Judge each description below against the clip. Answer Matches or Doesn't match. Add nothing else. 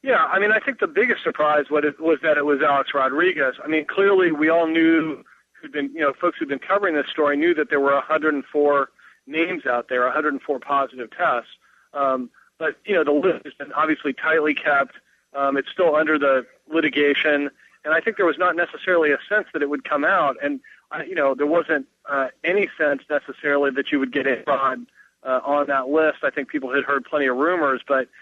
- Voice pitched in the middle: Matches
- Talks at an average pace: Doesn't match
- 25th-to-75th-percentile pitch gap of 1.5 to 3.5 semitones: Matches